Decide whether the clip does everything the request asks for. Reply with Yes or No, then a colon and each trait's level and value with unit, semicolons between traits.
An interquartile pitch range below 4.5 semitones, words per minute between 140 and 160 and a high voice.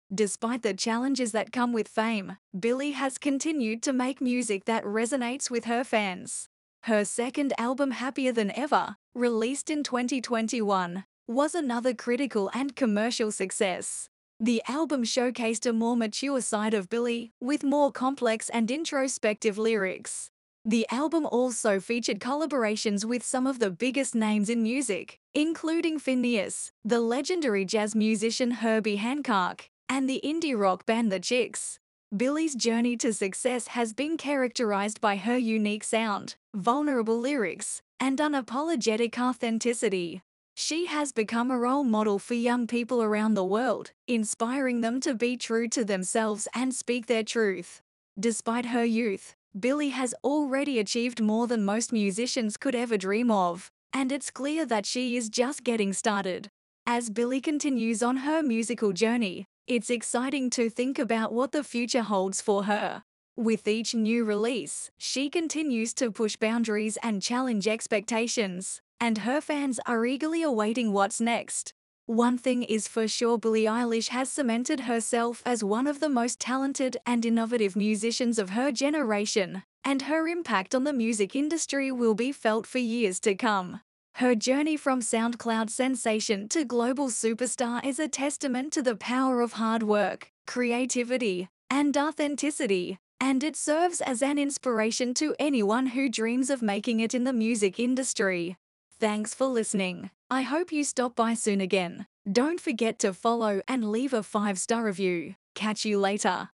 Yes: average, 3.1 semitones; average, 155 wpm; high, 235 Hz